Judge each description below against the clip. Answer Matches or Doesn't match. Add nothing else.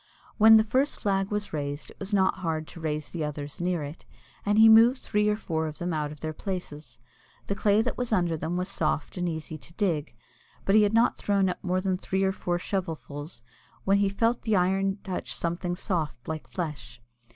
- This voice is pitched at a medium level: Matches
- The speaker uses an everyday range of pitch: Matches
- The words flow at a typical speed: Doesn't match